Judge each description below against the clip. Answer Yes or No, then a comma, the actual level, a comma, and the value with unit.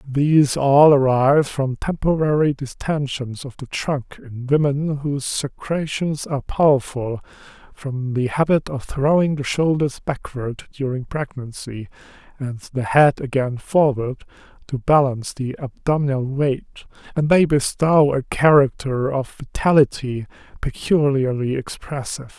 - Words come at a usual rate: No, slow, 120 wpm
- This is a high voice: No, medium, 140 Hz